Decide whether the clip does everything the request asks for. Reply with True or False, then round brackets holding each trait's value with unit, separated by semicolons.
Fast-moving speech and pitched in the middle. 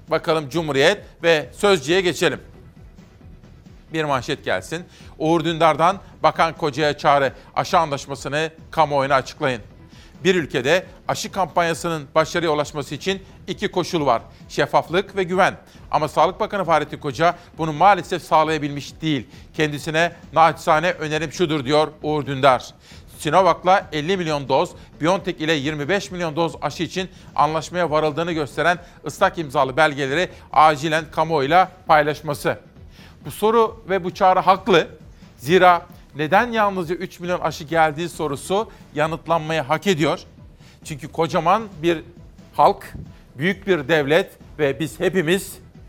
False (120 wpm; 160 Hz)